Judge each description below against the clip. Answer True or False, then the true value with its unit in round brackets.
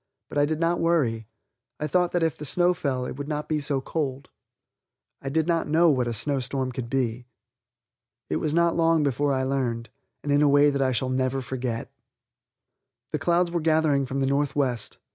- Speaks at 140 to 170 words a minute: False (200 wpm)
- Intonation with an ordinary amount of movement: True (3.4 semitones)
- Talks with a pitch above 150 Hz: False (140 Hz)